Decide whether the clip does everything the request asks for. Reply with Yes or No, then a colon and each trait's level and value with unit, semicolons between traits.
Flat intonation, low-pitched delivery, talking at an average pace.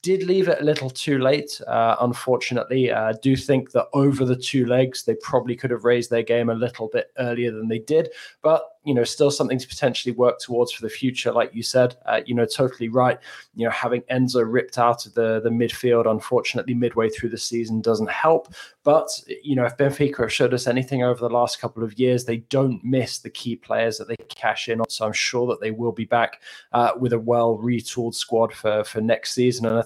No: narrow, 2.0 semitones; low, 120 Hz; fast, 230 wpm